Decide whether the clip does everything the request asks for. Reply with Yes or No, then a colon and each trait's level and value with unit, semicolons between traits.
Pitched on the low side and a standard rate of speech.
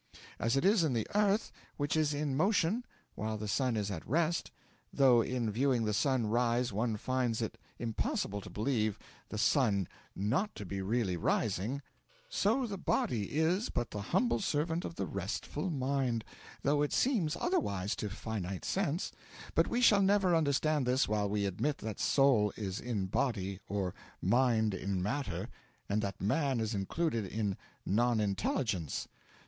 Yes: low, 120 Hz; average, 160 wpm